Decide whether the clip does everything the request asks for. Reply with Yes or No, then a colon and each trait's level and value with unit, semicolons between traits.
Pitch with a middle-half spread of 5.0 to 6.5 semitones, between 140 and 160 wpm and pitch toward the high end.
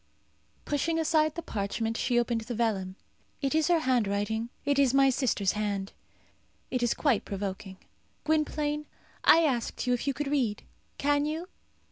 Yes: wide, 5.4 semitones; average, 155 wpm; very high, 255 Hz